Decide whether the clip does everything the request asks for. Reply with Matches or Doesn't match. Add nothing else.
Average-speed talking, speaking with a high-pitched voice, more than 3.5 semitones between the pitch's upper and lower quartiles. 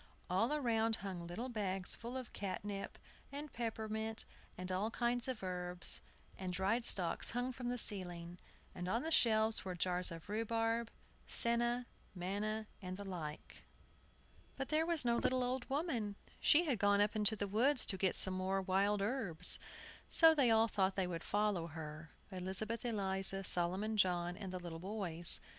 Matches